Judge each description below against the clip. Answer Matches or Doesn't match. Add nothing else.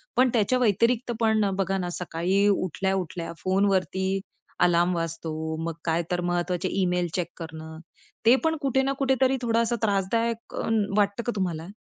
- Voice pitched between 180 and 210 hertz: Matches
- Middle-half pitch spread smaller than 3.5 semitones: Doesn't match